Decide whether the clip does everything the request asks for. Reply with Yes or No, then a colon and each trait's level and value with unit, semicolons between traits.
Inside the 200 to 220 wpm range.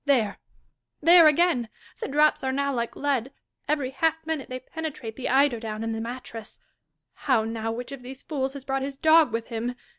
Yes: fast, 205 wpm